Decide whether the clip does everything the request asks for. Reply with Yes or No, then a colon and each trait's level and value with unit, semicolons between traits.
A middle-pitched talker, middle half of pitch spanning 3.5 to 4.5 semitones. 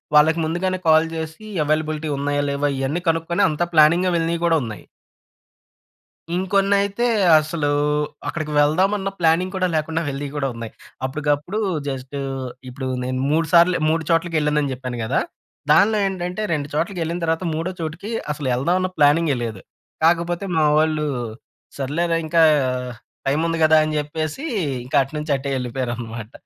No: medium, 155 Hz; average, 3.1 semitones